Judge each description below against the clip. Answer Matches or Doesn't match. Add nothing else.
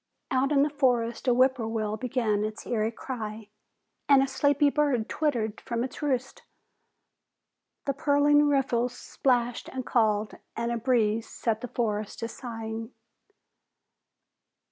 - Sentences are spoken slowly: Matches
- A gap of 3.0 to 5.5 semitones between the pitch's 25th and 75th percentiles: Matches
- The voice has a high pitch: Matches